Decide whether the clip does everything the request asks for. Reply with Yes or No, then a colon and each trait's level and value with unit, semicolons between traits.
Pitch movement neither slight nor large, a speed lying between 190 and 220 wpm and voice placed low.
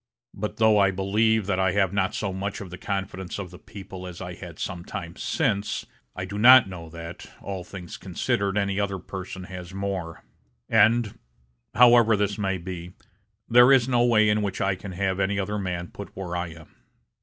No: narrow, 2.2 semitones; average, 195 wpm; very low, 95 Hz